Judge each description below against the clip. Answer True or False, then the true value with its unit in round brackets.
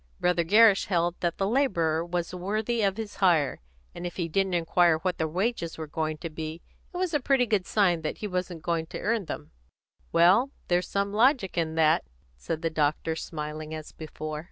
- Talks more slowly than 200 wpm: False (205 wpm)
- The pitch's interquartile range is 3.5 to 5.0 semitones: True (3.9 semitones)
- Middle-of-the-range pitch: True (175 Hz)